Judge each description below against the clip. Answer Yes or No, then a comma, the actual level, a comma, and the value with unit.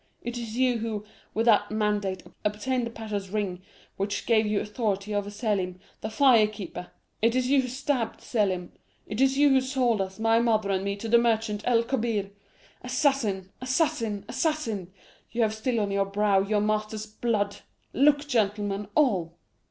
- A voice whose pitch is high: Yes, high, 215 Hz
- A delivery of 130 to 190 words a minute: Yes, average, 170 wpm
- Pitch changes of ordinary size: Yes, average, 3.0 semitones